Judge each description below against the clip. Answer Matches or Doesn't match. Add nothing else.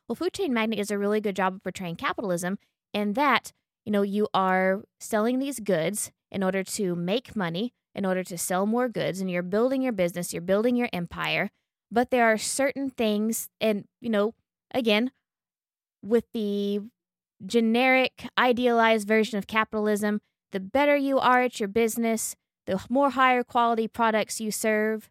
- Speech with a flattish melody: Doesn't match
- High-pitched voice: Matches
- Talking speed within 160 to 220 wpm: Matches